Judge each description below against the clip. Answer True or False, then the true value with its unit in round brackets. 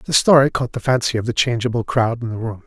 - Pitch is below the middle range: True (120 Hz)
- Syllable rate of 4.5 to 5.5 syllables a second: False (6.1 syllables/s)